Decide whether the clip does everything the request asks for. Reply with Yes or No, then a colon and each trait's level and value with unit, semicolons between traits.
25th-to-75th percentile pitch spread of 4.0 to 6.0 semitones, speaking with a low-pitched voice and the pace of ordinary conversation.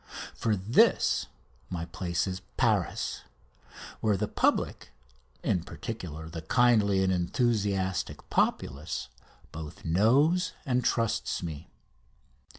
No: wide, 5.4 semitones; very low, 95 Hz; slow, 100 wpm